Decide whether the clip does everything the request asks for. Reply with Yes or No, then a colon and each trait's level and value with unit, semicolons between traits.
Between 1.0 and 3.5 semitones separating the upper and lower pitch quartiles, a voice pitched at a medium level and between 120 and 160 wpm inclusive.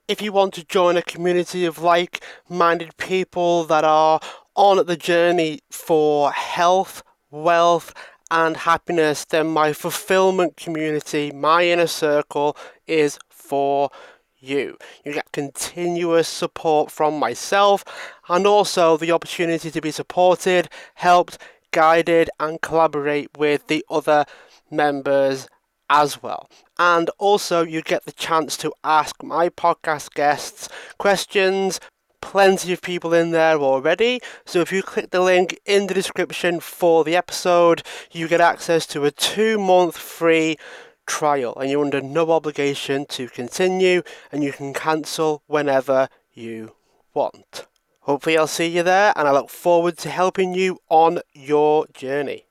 Yes: average, 2.9 semitones; medium, 165 Hz; average, 140 wpm